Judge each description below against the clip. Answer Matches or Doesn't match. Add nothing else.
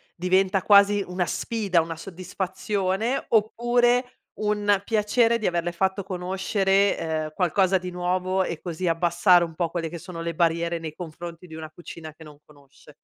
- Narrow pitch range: Doesn't match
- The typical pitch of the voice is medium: Matches